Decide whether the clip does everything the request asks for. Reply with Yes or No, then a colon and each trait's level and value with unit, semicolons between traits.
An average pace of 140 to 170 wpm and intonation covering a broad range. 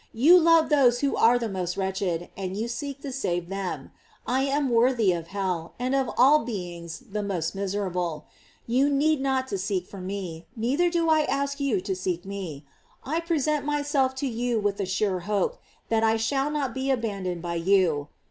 No: average, 190 wpm; wide, 6.7 semitones